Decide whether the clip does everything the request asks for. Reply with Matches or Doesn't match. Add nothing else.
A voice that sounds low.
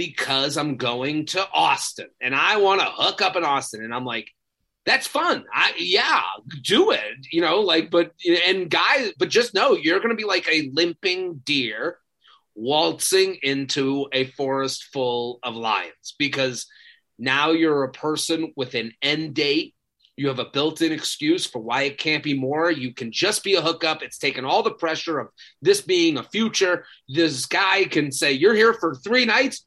Doesn't match